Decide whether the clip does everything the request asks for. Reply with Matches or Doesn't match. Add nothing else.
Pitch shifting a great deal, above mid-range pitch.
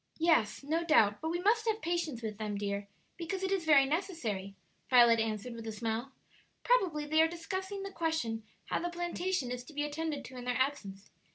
Matches